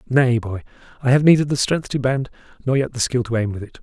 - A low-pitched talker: Yes, low, 125 Hz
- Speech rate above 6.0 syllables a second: Yes, 6.2 syllables/s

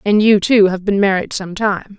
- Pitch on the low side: No, high, 200 Hz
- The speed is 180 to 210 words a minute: No, fast, 240 wpm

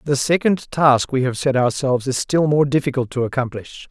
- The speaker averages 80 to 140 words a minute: No, average, 200 wpm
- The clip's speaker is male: Yes, male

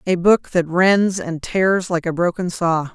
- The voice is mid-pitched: Yes, medium, 175 Hz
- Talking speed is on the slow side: No, fast, 205 wpm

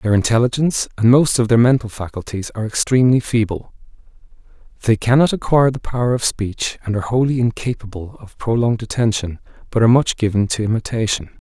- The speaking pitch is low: Yes, low, 115 Hz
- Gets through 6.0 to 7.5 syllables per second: Yes, 6.3 syllables/s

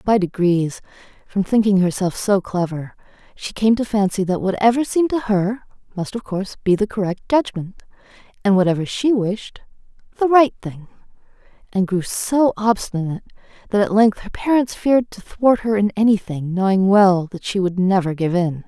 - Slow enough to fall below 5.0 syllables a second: No, 5.1 syllables/s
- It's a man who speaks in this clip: No, female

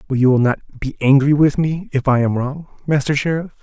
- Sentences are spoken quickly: Yes, fast, 230 wpm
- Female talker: No, male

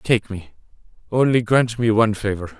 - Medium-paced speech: Yes, average, 160 wpm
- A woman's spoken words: No, male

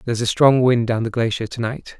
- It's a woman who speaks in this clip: No, male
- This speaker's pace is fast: Yes, fast, 300 wpm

